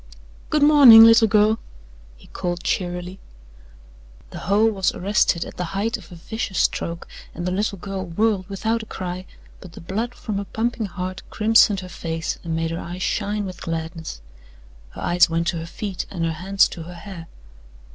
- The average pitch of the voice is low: No, medium, 185 Hz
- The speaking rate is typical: Yes, average, 185 wpm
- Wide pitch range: No, average, 3.7 semitones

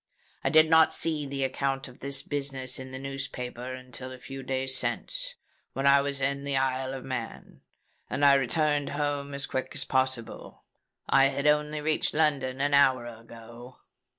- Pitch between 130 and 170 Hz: Yes, low, 135 Hz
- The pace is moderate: Yes, average, 170 wpm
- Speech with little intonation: Yes, narrow, 1.6 semitones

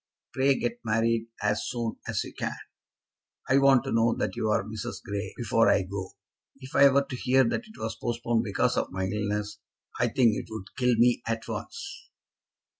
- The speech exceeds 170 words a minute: Yes, average, 190 wpm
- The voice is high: No, low, 115 Hz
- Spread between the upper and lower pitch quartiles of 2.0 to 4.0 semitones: Yes, average, 3.1 semitones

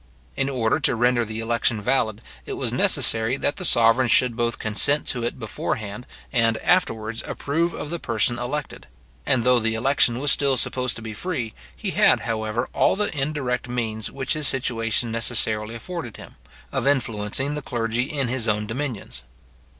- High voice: No, low, 120 Hz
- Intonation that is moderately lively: Yes, average, 3.2 semitones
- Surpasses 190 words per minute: No, average, 175 wpm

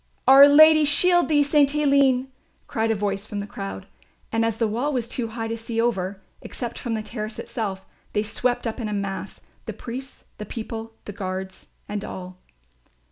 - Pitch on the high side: Yes, high, 225 Hz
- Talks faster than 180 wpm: Yes, average, 190 wpm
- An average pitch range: Yes, average, 4.4 semitones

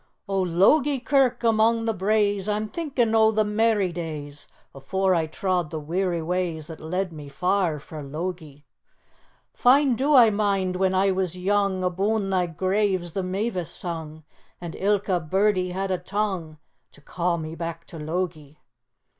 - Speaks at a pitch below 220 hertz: Yes, medium, 185 Hz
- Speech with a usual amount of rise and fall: Yes, average, 3.9 semitones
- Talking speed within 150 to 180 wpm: Yes, average, 155 wpm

